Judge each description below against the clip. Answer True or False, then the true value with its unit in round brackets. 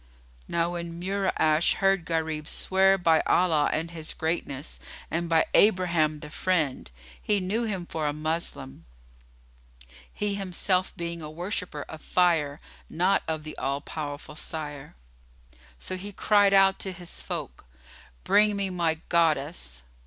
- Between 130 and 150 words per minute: True (140 wpm)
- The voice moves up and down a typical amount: True (3.4 semitones)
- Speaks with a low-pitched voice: False (170 Hz)